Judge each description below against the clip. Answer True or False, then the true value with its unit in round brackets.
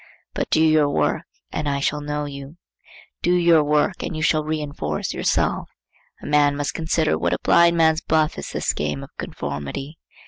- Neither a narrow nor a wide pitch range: False (2.3 semitones)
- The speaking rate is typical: True (175 wpm)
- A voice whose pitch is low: False (150 Hz)